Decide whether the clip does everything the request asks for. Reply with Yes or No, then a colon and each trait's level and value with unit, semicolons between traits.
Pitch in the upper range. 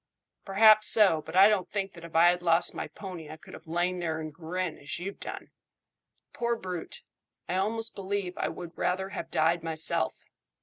No: medium, 180 Hz